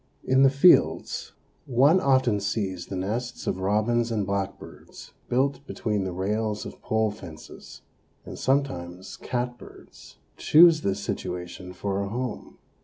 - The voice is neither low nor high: No, low, 110 Hz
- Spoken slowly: Yes, slow, 130 wpm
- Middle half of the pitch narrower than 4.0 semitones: No, average, 5.0 semitones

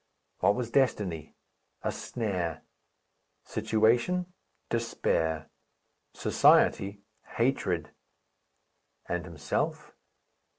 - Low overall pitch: Yes, low, 105 Hz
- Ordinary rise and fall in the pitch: No, wide, 5.8 semitones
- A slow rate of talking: Yes, slow, 60 wpm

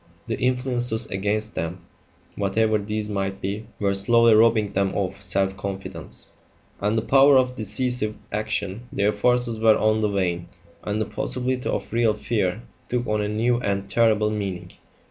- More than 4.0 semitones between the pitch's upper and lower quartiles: No, average, 2.9 semitones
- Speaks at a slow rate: No, average, 160 wpm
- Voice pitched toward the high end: No, low, 105 Hz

